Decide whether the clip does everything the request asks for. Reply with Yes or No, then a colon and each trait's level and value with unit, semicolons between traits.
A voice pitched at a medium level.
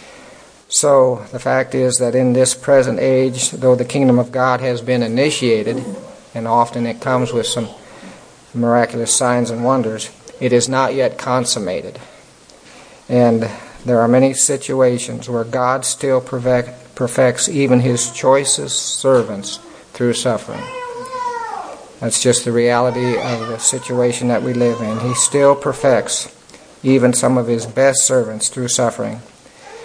No: low, 125 Hz